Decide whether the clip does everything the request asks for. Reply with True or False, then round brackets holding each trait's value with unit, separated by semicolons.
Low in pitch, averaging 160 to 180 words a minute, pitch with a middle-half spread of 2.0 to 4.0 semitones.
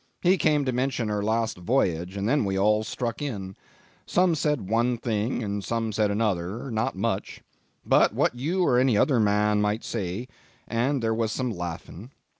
True (115 Hz; 170 wpm; 3.6 semitones)